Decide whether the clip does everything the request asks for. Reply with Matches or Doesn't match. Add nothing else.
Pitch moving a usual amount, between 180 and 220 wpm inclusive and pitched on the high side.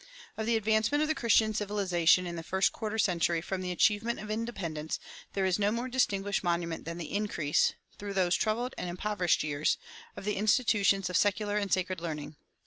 Matches